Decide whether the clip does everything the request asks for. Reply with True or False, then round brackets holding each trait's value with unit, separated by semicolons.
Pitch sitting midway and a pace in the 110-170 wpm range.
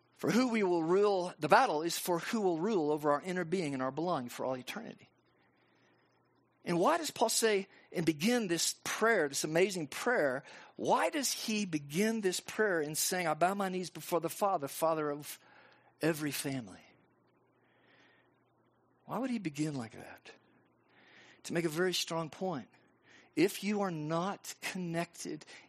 True (175 Hz; 165 wpm)